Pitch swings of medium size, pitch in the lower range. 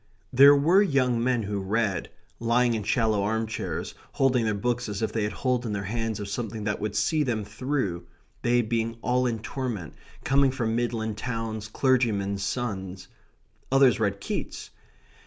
Yes: average, 3.1 semitones; low, 115 Hz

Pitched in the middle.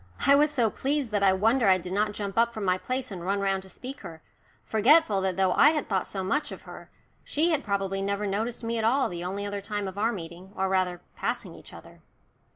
No: high, 200 Hz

